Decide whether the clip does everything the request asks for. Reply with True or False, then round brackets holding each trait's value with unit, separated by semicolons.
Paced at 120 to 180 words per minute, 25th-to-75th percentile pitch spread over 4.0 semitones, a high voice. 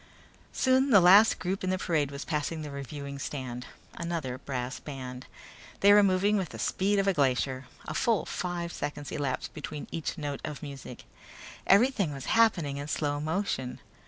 False (170 wpm; 5.3 semitones; 150 Hz)